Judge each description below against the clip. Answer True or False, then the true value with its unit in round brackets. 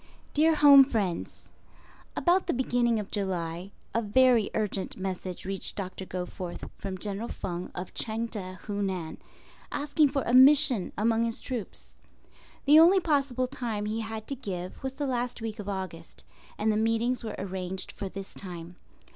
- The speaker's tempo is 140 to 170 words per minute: True (160 wpm)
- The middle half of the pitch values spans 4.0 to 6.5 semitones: True (5.2 semitones)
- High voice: True (220 Hz)